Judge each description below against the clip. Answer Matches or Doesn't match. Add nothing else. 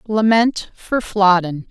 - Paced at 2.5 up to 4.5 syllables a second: Matches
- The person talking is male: Doesn't match